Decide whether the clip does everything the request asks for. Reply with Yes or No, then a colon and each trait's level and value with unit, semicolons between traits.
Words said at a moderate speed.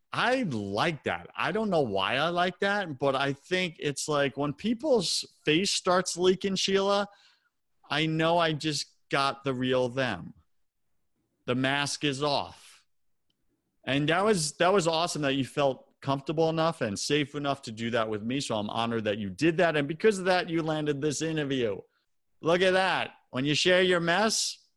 Yes: average, 180 wpm